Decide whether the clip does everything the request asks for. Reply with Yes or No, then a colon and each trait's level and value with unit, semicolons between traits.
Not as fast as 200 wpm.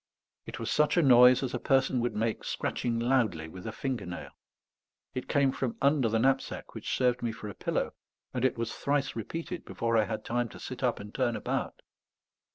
No: fast, 205 wpm